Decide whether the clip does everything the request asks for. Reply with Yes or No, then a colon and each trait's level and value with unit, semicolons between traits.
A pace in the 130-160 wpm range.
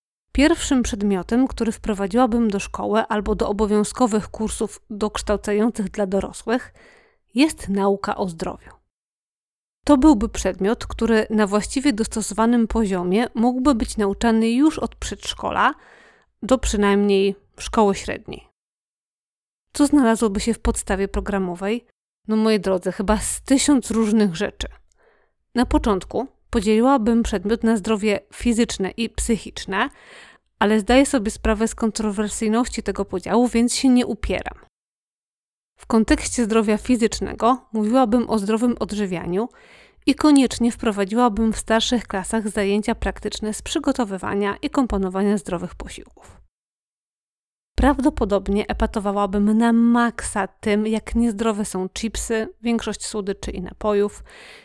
No: average, 115 wpm